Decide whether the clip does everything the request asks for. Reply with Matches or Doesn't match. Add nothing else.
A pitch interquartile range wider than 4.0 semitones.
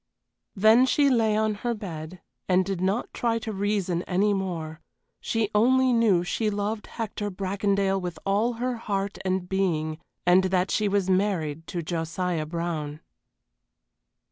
Doesn't match